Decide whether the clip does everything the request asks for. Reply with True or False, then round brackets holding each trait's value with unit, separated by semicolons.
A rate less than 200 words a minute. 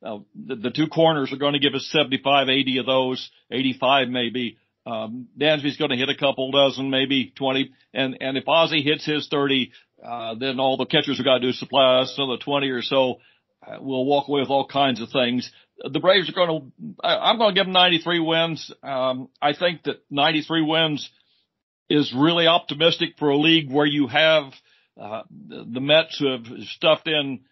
False (205 wpm)